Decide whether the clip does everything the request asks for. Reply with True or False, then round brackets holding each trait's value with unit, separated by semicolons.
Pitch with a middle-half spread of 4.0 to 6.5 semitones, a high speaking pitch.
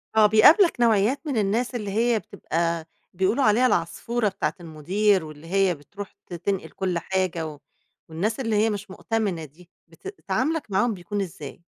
True (4.5 semitones; 195 Hz)